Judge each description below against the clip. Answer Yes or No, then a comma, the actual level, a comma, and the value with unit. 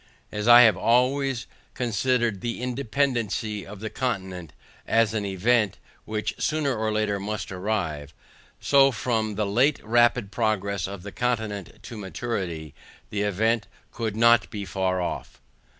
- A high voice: No, low, 110 Hz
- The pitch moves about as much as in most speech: Yes, average, 3.2 semitones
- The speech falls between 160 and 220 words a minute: No, average, 140 wpm